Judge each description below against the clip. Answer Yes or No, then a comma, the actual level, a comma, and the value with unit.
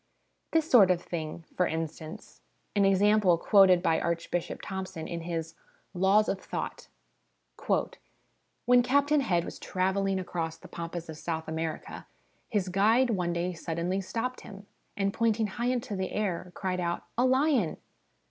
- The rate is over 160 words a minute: No, average, 155 wpm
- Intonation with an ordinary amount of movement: Yes, average, 3.9 semitones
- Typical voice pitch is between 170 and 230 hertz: Yes, medium, 185 Hz